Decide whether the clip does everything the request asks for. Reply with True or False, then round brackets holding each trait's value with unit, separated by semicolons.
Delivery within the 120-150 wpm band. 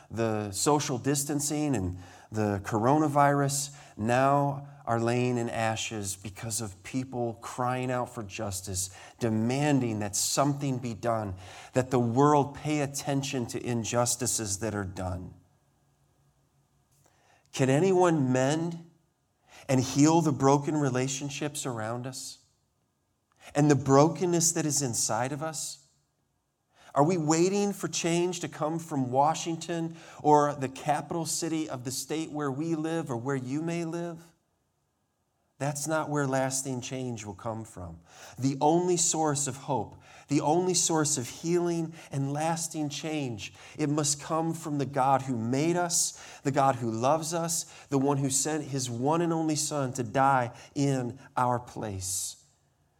True (140 wpm)